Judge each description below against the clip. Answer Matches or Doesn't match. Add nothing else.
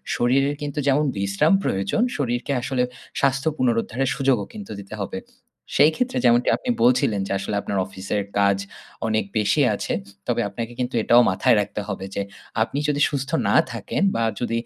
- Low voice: Matches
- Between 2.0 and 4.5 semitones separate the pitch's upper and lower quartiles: Doesn't match